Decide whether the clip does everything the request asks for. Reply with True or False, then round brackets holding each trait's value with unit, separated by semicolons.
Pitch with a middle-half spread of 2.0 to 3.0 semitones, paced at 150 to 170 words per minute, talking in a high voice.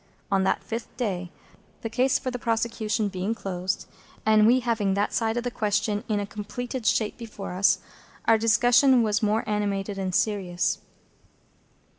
True (2.7 semitones; 160 wpm; 215 Hz)